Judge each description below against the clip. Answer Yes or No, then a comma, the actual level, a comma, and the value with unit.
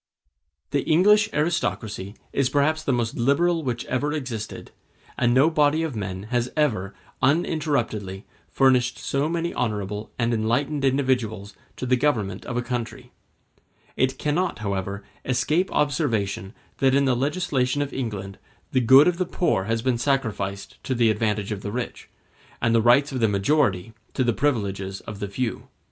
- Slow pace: No, average, 160 wpm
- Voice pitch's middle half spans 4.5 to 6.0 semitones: Yes, average, 5.2 semitones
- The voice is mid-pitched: No, low, 125 Hz